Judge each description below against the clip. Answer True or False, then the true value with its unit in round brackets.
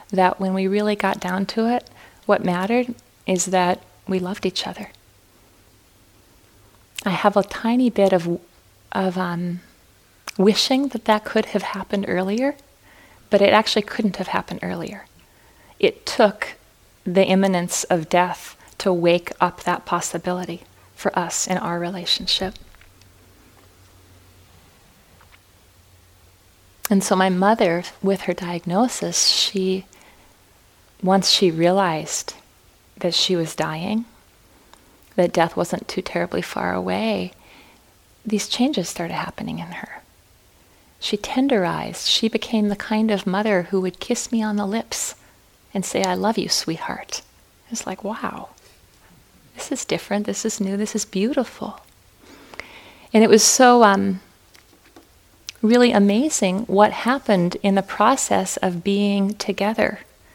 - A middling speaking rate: False (130 wpm)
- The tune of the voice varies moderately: True (3.5 semitones)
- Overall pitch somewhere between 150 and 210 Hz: True (190 Hz)